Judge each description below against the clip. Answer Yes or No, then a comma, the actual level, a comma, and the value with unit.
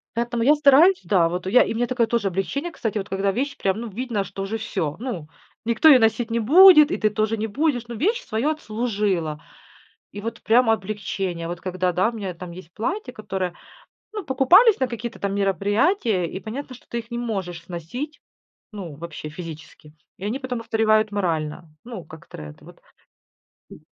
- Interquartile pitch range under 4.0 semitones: No, average, 5.0 semitones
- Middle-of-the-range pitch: No, high, 215 Hz